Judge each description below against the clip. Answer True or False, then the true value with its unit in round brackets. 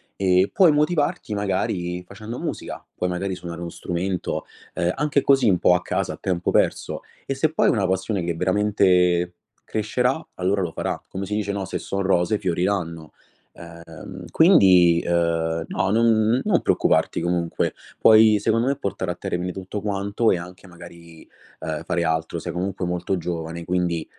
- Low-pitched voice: True (95 Hz)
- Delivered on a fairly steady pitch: False (3.3 semitones)